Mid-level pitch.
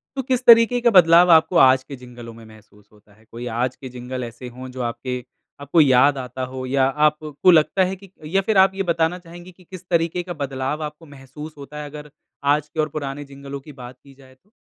Yes: medium, 145 Hz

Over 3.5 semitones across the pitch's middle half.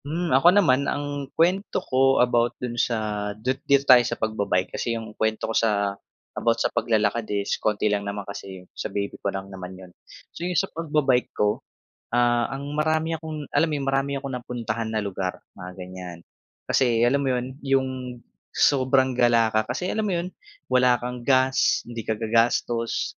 Yes: average, 4.2 semitones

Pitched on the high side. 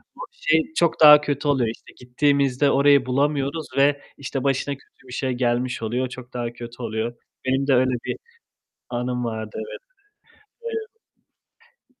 No: low, 130 Hz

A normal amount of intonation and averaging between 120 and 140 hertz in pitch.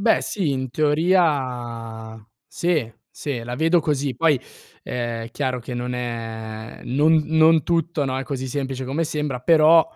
Yes: average, 4.5 semitones; low, 135 Hz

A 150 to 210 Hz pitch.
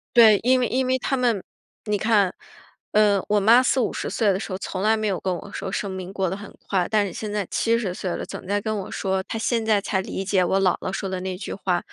Yes: high, 200 Hz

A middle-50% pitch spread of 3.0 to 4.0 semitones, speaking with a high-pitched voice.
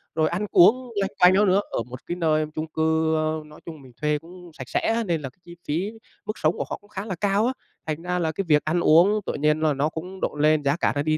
No: average, 3.3 semitones; medium, 160 Hz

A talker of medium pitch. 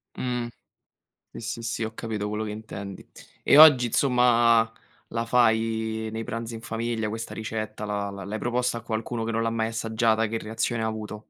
No: low, 115 Hz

